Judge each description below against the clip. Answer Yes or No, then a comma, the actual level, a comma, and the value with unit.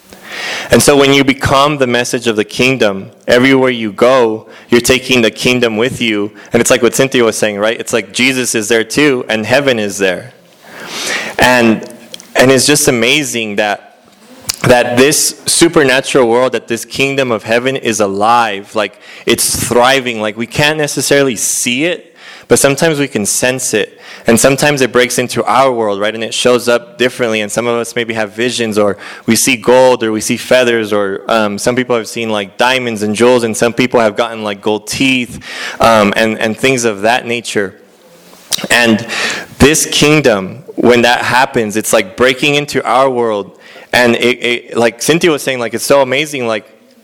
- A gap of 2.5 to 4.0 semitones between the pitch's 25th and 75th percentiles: Yes, average, 2.9 semitones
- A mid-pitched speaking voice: No, low, 120 Hz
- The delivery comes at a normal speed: Yes, average, 185 wpm